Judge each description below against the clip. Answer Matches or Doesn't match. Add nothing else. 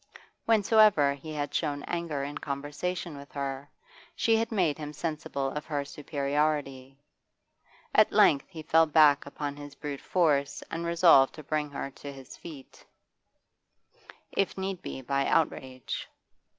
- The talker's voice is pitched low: Doesn't match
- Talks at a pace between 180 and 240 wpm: Doesn't match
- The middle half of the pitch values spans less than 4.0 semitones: Matches